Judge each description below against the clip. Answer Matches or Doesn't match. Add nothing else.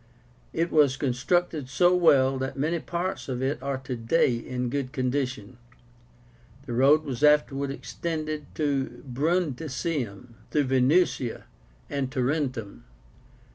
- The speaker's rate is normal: Doesn't match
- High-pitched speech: Doesn't match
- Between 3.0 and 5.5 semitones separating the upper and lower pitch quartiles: Matches